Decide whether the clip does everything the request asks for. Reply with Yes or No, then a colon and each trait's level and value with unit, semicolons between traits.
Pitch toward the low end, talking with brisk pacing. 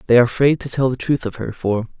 Yes: low, 125 Hz; fast, 300 wpm